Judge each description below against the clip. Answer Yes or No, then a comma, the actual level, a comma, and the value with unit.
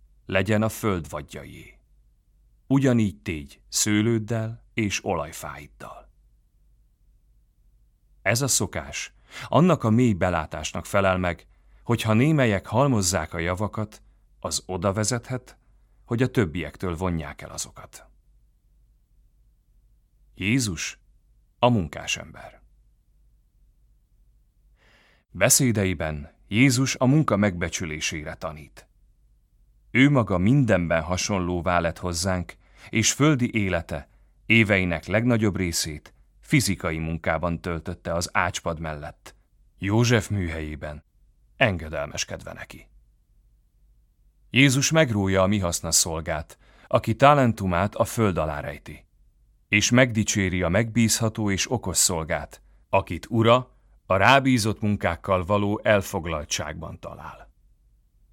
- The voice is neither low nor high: No, low, 100 Hz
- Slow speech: Yes, slow, 95 wpm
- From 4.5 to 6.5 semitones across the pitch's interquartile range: Yes, average, 4.9 semitones